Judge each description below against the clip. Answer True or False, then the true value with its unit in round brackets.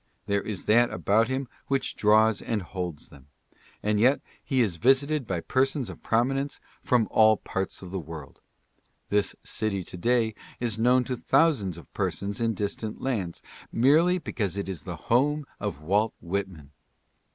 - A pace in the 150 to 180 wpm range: True (165 wpm)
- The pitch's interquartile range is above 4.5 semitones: True (5.0 semitones)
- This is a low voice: True (110 Hz)